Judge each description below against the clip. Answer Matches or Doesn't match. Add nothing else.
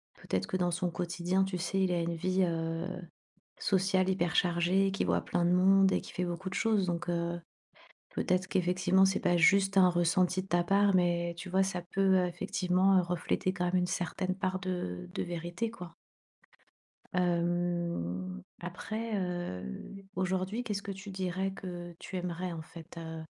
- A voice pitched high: Doesn't match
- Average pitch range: Doesn't match